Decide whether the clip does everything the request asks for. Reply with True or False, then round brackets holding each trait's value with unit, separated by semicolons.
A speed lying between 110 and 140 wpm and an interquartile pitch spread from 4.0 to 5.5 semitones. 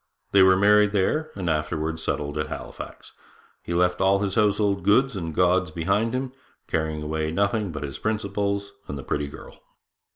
False (170 wpm; 4.5 semitones)